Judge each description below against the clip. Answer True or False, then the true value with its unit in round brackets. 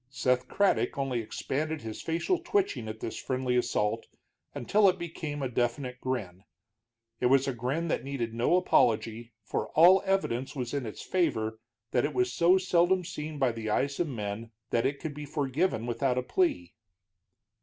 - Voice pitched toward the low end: True (130 Hz)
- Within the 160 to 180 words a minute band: True (175 wpm)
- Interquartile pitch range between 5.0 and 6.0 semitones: True (5.6 semitones)